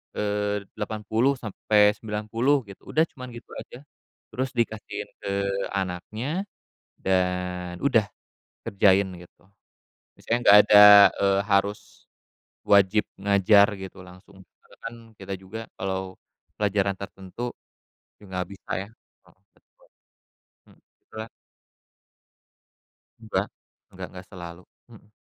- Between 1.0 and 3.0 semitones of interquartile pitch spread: Yes, narrow, 2.6 semitones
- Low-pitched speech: Yes, low, 100 Hz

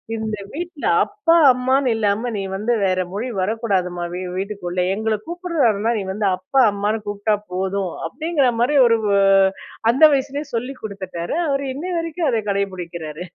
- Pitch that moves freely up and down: Yes, wide, 6.1 semitones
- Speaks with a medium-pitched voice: No, high, 220 Hz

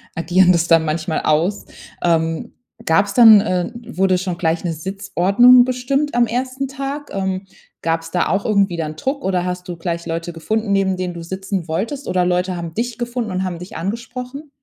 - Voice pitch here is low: No, high, 190 Hz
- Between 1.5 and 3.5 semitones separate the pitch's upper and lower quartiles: No, wide, 5.5 semitones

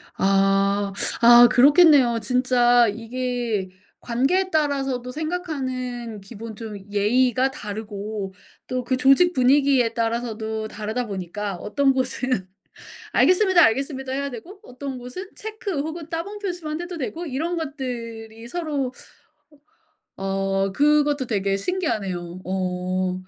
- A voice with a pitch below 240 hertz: No, very high, 250 Hz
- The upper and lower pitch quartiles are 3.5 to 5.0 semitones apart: No, wide, 5.5 semitones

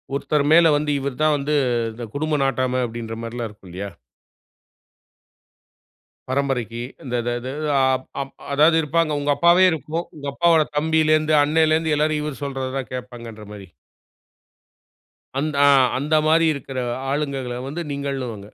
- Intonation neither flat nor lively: Yes, average, 3.6 semitones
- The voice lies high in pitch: No, medium, 140 Hz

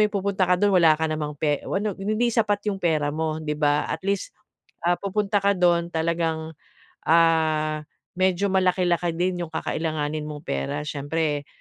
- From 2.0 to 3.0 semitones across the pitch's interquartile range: No, average, 3.5 semitones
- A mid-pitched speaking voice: Yes, medium, 170 Hz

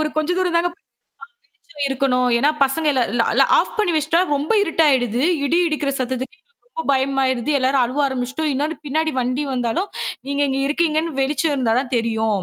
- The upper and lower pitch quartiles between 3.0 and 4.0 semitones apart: Yes, average, 3.7 semitones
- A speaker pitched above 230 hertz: Yes, very high, 275 Hz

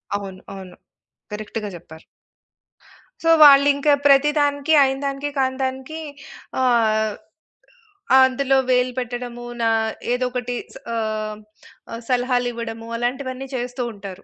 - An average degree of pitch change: Yes, average, 3.1 semitones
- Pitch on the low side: No, high, 245 Hz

